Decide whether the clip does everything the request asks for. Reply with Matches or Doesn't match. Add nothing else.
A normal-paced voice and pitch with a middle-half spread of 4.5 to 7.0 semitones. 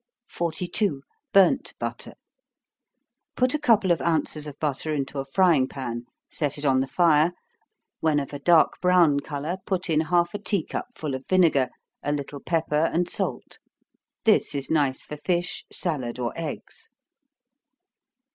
Doesn't match